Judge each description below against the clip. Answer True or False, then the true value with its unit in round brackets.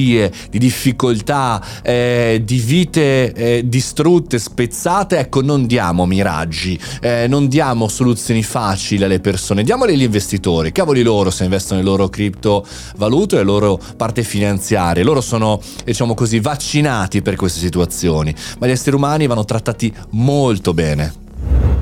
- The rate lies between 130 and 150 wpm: True (140 wpm)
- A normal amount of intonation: True (4.7 semitones)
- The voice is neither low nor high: False (110 Hz)